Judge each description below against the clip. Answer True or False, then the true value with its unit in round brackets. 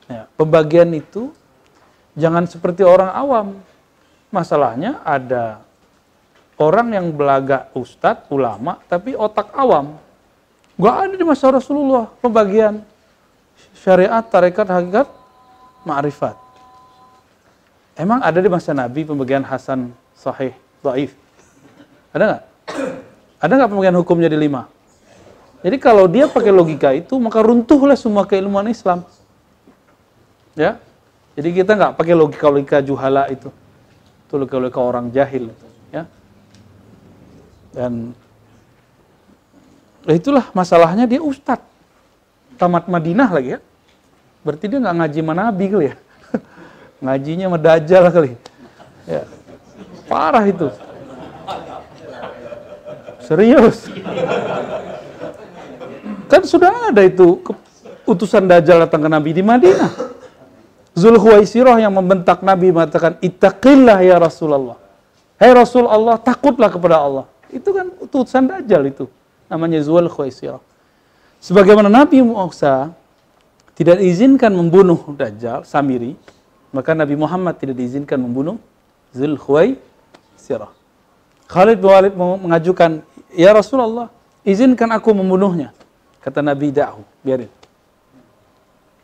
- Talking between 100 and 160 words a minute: True (105 wpm)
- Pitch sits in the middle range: True (175 Hz)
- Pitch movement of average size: False (8.1 semitones)